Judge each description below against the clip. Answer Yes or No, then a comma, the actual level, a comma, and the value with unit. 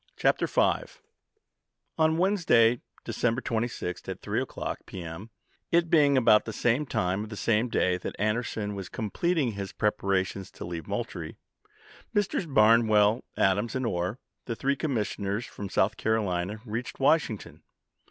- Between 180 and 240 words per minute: No, average, 150 wpm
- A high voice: No, low, 110 Hz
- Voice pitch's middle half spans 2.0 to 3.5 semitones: No, average, 4.5 semitones